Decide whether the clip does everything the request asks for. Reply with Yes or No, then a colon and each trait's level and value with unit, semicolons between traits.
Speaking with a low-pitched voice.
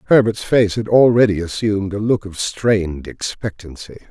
Yes: low, 105 Hz